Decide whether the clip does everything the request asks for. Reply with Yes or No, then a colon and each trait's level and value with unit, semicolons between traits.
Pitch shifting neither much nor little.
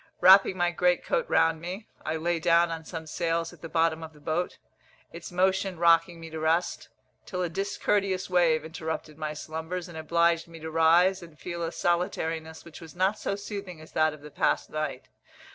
No: narrow, 1.9 semitones